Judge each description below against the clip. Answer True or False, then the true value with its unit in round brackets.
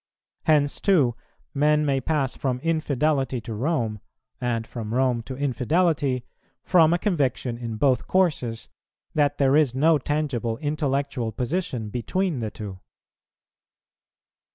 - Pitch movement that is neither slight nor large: True (4.2 semitones)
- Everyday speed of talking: False (125 wpm)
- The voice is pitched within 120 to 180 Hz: True (135 Hz)